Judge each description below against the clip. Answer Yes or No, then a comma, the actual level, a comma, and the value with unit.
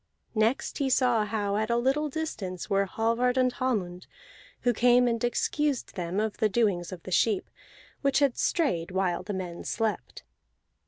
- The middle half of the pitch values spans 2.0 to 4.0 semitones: No, average, 4.7 semitones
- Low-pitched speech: No, high, 225 Hz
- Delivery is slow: No, average, 165 wpm